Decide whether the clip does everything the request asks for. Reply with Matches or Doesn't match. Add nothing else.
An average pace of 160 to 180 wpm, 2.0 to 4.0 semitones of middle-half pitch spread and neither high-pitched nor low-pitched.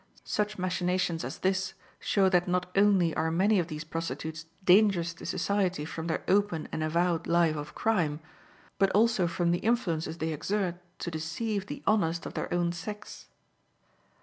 Matches